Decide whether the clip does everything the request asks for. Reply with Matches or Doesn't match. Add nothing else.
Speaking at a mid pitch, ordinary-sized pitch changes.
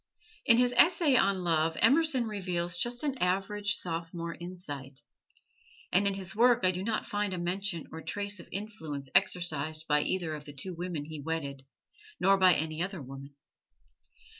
Matches